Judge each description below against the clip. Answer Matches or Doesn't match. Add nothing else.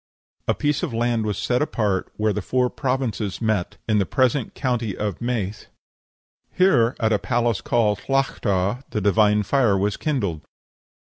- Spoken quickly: Doesn't match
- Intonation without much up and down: Doesn't match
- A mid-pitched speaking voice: Doesn't match